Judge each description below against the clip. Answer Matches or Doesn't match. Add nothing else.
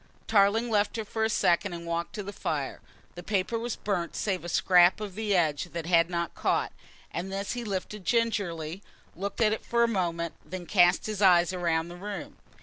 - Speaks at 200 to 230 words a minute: Matches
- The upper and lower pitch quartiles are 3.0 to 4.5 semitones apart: Matches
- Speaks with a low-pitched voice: Doesn't match